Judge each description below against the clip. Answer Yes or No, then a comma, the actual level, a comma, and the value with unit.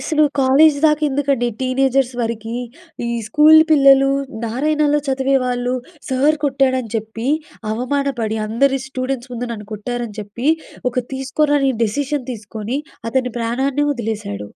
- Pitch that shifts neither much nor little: Yes, average, 3.1 semitones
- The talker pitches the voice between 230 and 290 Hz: Yes, very high, 260 Hz